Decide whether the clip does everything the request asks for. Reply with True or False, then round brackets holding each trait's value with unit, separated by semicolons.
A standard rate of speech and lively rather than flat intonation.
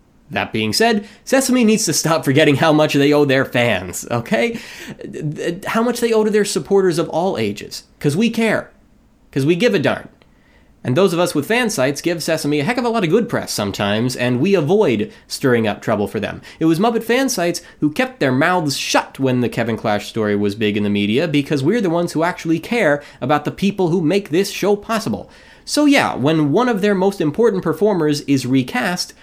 False (215 wpm; 7.4 semitones)